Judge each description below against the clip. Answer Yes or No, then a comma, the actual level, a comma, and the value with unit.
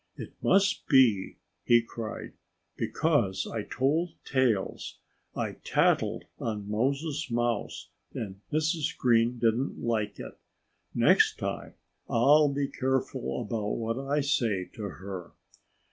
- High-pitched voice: No, low, 120 Hz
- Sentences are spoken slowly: Yes, slow, 115 wpm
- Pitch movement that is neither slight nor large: Yes, average, 4.4 semitones